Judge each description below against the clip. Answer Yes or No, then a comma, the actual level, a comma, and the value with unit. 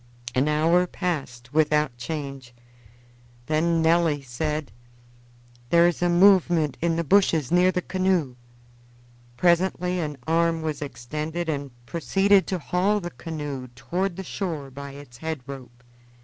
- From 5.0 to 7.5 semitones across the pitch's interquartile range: No, average, 3.8 semitones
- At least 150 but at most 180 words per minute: No, slow, 135 wpm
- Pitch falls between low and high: Yes, medium, 160 Hz